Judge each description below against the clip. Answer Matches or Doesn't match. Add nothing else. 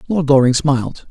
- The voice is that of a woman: Doesn't match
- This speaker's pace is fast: Doesn't match